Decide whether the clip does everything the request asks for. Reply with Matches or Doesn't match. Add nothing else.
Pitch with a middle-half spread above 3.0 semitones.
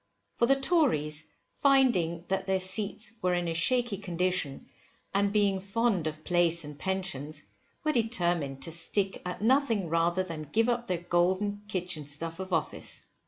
Matches